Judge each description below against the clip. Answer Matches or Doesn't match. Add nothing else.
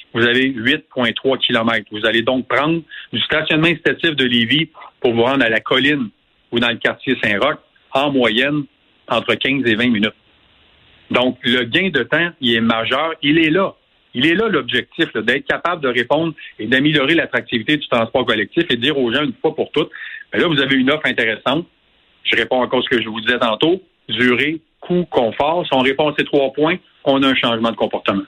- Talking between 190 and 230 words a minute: Matches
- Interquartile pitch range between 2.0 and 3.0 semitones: Doesn't match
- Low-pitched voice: Matches